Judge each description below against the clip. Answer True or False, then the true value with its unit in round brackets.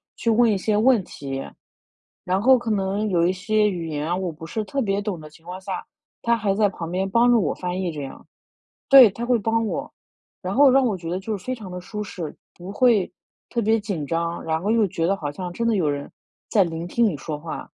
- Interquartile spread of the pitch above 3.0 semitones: True (4.7 semitones)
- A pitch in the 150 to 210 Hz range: True (195 Hz)